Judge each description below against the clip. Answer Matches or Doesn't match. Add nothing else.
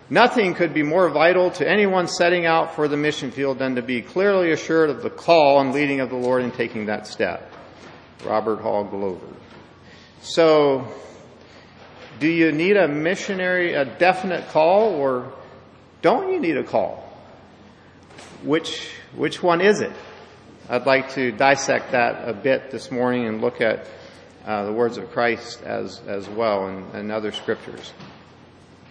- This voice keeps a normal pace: Matches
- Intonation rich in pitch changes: Matches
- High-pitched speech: Doesn't match